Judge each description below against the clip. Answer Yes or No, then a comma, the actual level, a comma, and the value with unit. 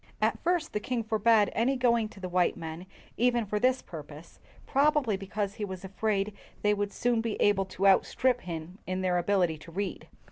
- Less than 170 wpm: No, average, 190 wpm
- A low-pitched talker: No, high, 205 Hz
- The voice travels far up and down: No, average, 3.9 semitones